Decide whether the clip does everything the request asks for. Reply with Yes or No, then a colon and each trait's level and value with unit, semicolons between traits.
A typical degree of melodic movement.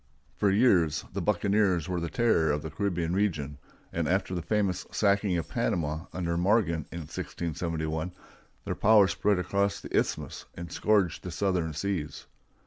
Yes: average, 3.6 semitones